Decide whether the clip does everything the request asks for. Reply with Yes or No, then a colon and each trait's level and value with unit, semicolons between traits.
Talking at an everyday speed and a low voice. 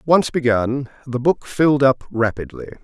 Yes: average, 150 wpm; low, 130 Hz